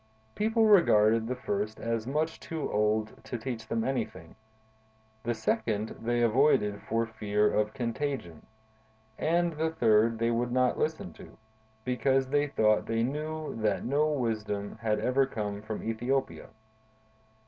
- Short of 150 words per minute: Yes, average, 140 wpm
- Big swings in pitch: No, average, 4.1 semitones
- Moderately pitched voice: No, low, 115 Hz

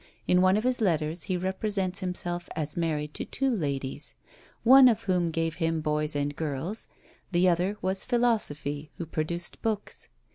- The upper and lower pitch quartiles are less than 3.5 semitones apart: No, average, 4.3 semitones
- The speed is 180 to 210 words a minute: No, average, 160 wpm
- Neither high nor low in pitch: Yes, medium, 175 Hz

